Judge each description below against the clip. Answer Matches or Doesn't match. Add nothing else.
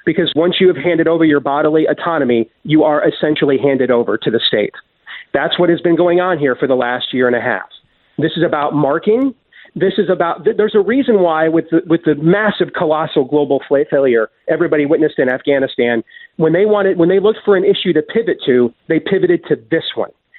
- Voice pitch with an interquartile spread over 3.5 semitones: Matches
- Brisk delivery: Matches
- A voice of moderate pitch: Matches